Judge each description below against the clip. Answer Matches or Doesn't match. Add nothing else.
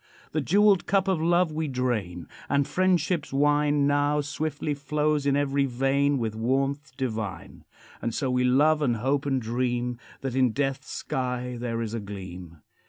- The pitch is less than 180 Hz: Matches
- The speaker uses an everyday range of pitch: Matches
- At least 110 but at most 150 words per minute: Doesn't match